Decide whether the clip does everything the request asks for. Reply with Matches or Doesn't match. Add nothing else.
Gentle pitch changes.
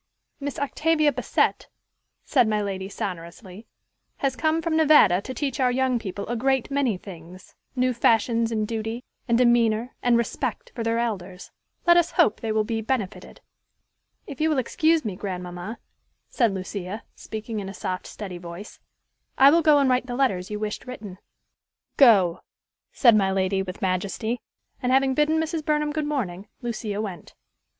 Doesn't match